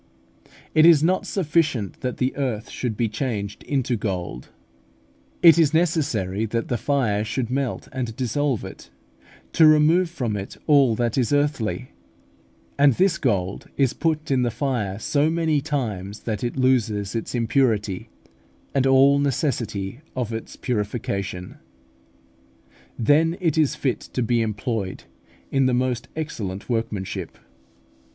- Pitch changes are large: No, average, 5.0 semitones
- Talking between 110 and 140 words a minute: Yes, slow, 135 wpm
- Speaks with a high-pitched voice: No, low, 125 Hz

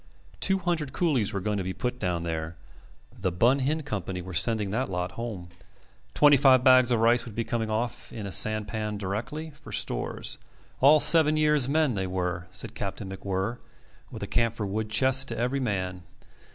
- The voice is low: Yes, low, 110 Hz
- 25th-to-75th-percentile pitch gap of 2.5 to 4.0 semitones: No, wide, 5.6 semitones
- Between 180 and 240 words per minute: Yes, average, 185 wpm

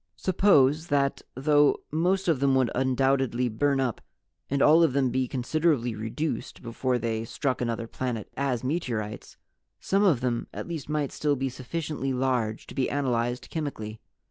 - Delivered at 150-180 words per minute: Yes, average, 160 wpm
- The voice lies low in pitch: Yes, low, 130 Hz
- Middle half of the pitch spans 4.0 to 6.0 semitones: No, average, 3.4 semitones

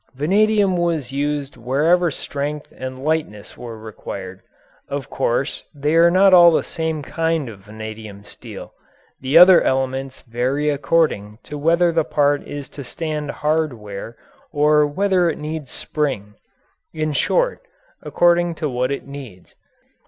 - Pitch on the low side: No, medium, 145 Hz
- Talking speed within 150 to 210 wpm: No, average, 140 wpm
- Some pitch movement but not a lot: Yes, average, 4.3 semitones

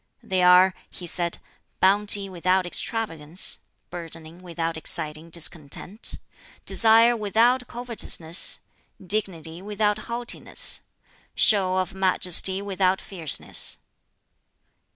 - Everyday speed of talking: No, slow, 90 wpm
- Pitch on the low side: No, medium, 185 Hz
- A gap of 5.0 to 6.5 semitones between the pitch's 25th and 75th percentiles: No, average, 3.6 semitones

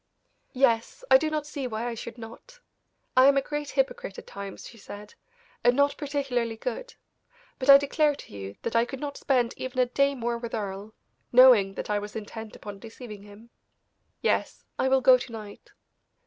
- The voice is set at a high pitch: Yes, high, 240 Hz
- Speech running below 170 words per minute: No, average, 190 wpm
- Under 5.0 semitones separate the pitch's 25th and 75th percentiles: Yes, average, 4.1 semitones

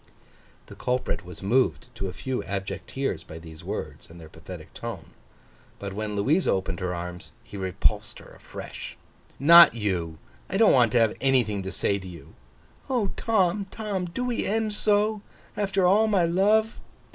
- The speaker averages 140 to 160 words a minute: No, average, 170 wpm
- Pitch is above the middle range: No, low, 125 Hz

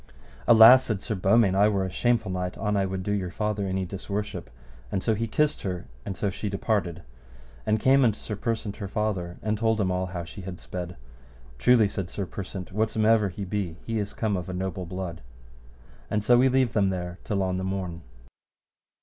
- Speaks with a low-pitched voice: Yes, low, 100 Hz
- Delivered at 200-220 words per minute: Yes, fast, 205 wpm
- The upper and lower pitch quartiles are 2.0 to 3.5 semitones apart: Yes, average, 2.8 semitones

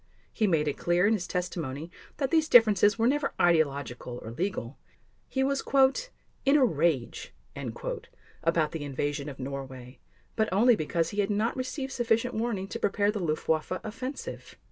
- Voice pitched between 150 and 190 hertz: Yes, medium, 185 Hz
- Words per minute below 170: Yes, average, 160 wpm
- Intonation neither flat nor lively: No, wide, 7.4 semitones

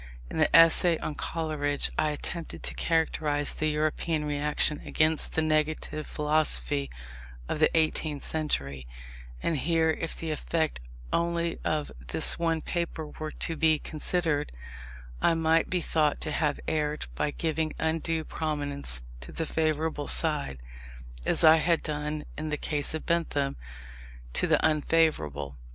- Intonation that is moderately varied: No, narrow, 1.6 semitones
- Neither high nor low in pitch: Yes, medium, 155 Hz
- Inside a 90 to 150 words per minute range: Yes, average, 140 wpm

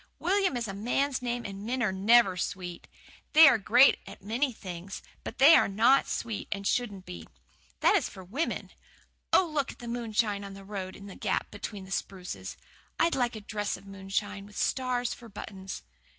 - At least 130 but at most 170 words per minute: No, average, 195 wpm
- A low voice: No, high, 210 Hz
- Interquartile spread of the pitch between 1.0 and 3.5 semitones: No, average, 4.0 semitones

